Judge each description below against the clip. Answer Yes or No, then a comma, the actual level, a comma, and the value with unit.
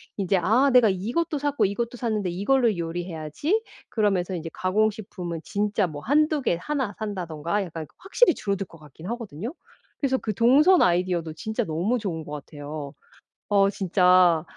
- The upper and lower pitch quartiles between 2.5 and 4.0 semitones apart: No, wide, 5.6 semitones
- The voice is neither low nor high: No, high, 200 Hz